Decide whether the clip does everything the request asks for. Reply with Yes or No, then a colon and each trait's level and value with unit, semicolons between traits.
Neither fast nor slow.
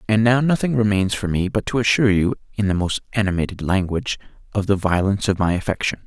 No: fast, 210 wpm